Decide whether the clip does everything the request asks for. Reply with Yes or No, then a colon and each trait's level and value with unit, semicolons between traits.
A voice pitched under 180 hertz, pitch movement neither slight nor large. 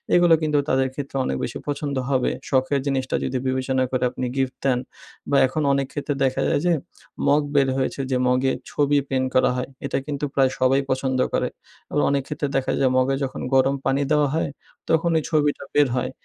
No: low, 135 Hz; narrow, 1.8 semitones